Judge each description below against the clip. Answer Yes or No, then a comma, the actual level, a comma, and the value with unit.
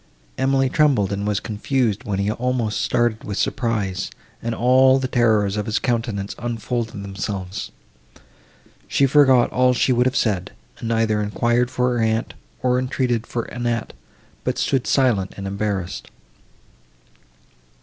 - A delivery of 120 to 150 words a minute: Yes, average, 140 wpm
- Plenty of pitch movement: No, average, 3.4 semitones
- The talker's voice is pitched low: Yes, low, 115 Hz